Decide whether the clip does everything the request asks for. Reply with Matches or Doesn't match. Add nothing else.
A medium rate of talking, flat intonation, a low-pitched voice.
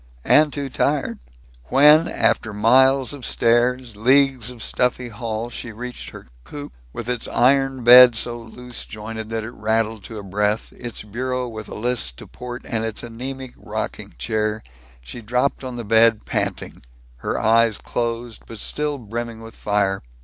Matches